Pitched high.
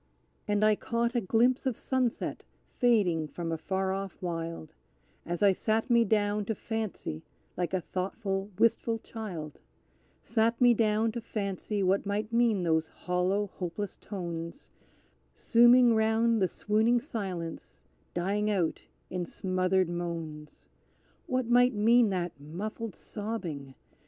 Yes: high, 205 Hz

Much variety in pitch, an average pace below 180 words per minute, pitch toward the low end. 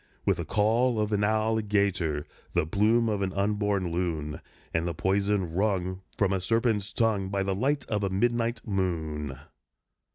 No: average, 2.9 semitones; average, 160 wpm; low, 100 Hz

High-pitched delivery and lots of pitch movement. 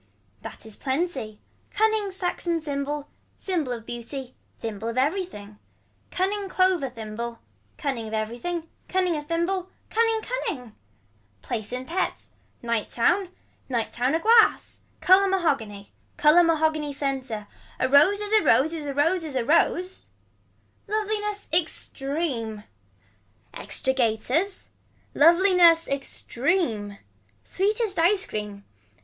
Yes: very high, 305 Hz; wide, 7.6 semitones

